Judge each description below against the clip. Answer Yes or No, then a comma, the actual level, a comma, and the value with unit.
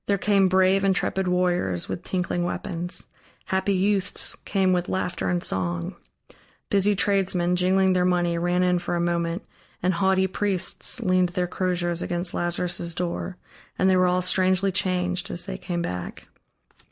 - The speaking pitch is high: No, medium, 180 Hz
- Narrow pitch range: Yes, narrow, 1.4 semitones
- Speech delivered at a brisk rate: No, average, 155 wpm